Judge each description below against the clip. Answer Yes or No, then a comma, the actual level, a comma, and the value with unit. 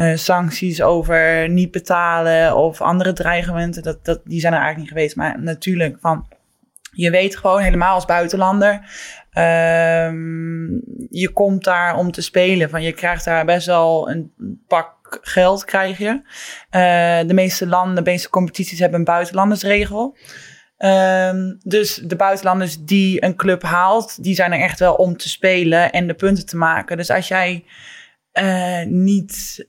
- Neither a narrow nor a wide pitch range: No, narrow, 2.2 semitones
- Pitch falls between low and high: Yes, medium, 180 Hz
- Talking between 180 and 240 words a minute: No, average, 160 wpm